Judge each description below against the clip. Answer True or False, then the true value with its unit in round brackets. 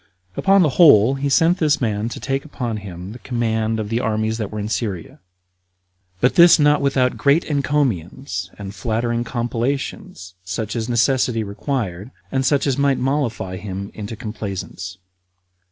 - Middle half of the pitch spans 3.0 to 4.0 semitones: False (4.8 semitones)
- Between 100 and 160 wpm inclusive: True (155 wpm)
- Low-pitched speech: True (115 Hz)